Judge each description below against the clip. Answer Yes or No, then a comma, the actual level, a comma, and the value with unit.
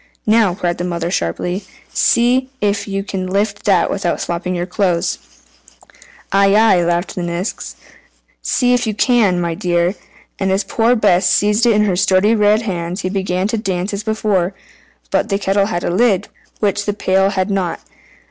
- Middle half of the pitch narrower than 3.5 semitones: Yes, average, 2.8 semitones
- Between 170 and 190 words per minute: Yes, average, 175 wpm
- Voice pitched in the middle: No, high, 195 Hz